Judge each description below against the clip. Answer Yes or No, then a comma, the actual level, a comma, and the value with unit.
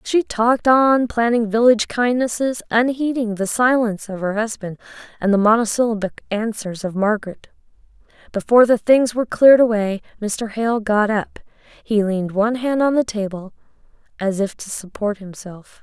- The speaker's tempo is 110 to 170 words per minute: Yes, average, 150 wpm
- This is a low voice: No, high, 220 Hz